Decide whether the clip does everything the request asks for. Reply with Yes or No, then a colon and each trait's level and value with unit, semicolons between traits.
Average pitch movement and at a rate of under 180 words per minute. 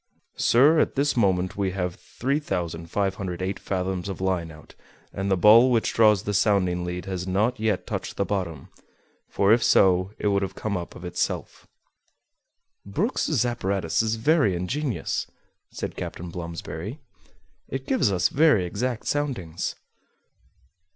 Yes: average, 4.2 semitones; average, 140 wpm